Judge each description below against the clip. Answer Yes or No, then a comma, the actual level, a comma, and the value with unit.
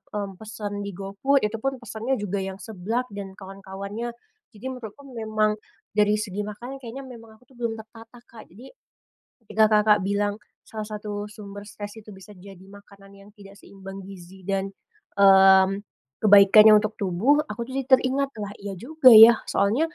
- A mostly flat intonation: Yes, narrow, 2.3 semitones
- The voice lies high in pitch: Yes, high, 210 Hz